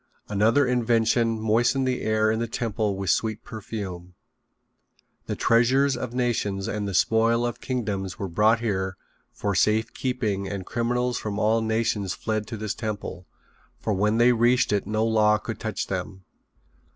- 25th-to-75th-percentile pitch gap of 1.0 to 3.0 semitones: Yes, narrow, 2.4 semitones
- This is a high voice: No, low, 110 Hz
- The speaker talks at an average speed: Yes, average, 160 wpm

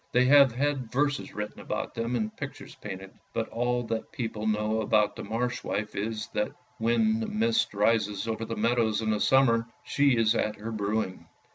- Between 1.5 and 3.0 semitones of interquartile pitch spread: Yes, narrow, 2.6 semitones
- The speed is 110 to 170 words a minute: No, average, 185 wpm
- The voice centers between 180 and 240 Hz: No, low, 115 Hz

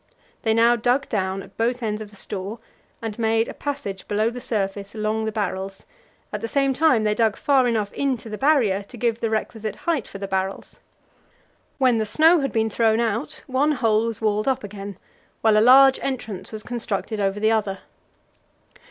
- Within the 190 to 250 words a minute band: Yes, average, 195 wpm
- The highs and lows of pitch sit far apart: No, average, 3.0 semitones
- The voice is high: Yes, high, 220 Hz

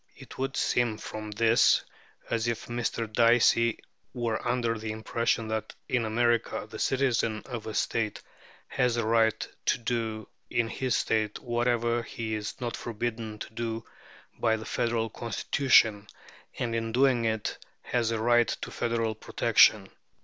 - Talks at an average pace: Yes, average, 150 wpm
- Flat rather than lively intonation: Yes, narrow, 1.3 semitones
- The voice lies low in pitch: Yes, low, 115 Hz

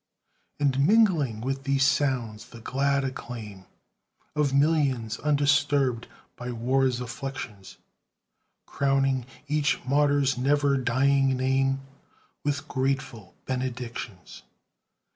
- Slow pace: Yes, slow, 90 wpm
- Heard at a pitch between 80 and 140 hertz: Yes, low, 135 Hz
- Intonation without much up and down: Yes, narrow, 2.3 semitones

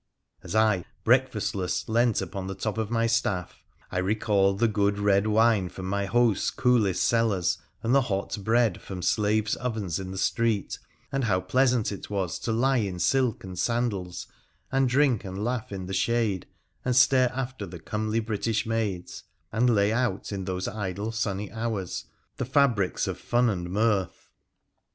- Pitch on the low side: Yes, low, 110 Hz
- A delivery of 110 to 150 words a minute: No, average, 170 wpm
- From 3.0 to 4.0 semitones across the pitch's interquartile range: Yes, average, 3.4 semitones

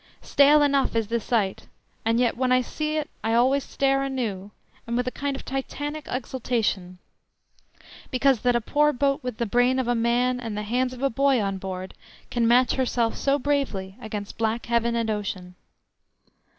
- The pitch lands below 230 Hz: No, high, 245 Hz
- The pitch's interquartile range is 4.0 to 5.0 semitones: No, average, 3.3 semitones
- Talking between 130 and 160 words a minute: No, average, 185 wpm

